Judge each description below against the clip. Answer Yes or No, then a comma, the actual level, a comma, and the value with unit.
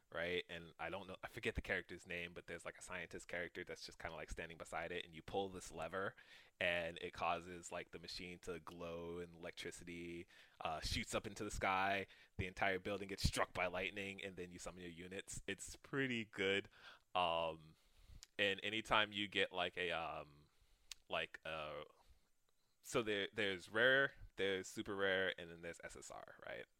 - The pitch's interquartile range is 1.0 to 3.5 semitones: Yes, narrow, 2.4 semitones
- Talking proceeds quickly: No, average, 180 wpm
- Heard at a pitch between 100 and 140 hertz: No, very low, 90 Hz